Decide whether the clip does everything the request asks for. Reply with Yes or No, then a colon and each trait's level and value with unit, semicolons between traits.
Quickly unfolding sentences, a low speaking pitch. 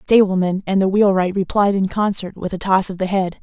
No: fast, 245 wpm; high, 190 Hz